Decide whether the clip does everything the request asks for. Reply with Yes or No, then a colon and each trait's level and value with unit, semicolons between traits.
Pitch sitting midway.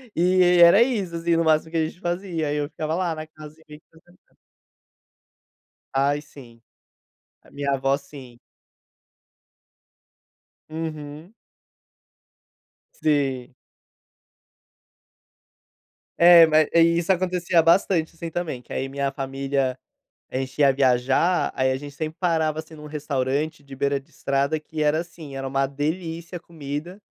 Yes: medium, 155 Hz